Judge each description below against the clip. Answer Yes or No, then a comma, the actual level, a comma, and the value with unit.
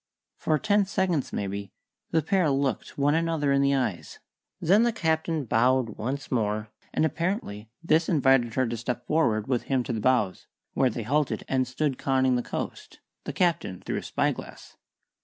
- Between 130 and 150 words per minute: No, average, 175 wpm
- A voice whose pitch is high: No, low, 135 Hz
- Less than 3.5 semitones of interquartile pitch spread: No, average, 4.9 semitones